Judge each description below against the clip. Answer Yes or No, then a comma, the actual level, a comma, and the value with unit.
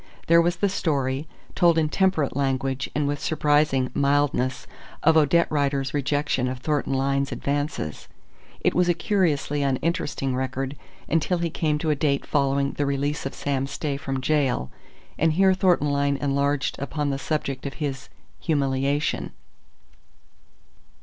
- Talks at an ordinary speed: Yes, average, 145 wpm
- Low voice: No, medium, 145 Hz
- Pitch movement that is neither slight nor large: No, narrow, 2.2 semitones